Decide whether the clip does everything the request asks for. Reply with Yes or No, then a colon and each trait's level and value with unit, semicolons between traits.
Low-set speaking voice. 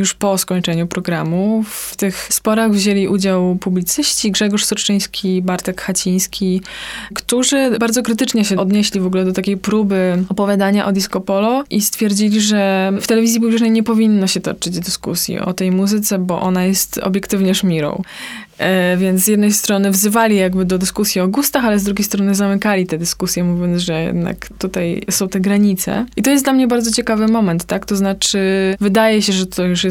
No: high, 200 Hz